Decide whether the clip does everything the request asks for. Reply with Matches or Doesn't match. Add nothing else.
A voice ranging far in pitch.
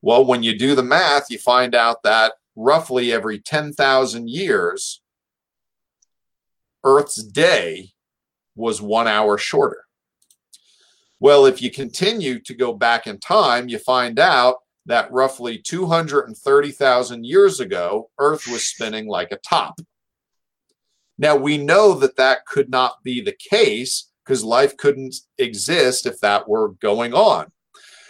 Matches